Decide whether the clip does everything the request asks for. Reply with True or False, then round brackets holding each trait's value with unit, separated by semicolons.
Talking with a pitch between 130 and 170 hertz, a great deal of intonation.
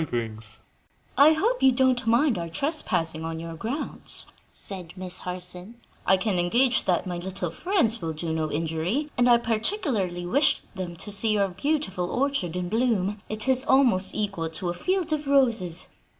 False (200 Hz; 6.9 semitones)